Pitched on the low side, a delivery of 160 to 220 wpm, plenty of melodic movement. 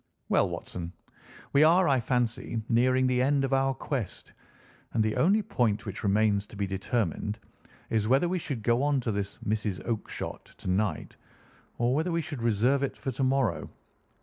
No: low, 120 Hz; average, 175 wpm; average, 4.5 semitones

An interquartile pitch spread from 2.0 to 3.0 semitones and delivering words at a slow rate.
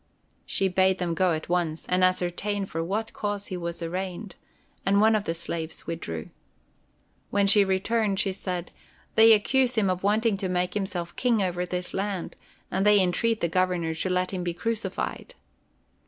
No: average, 2.7 semitones; average, 175 wpm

